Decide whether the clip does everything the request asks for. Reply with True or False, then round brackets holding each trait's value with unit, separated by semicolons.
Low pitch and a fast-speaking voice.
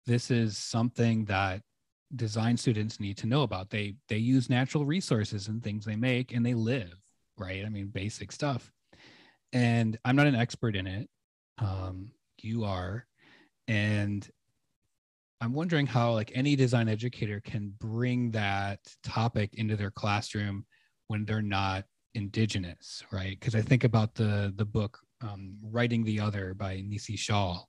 False (110 Hz; 155 wpm)